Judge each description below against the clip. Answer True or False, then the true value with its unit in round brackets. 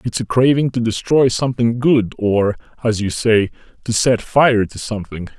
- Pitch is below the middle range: True (115 Hz)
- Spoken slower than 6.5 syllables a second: True (4.8 syllables/s)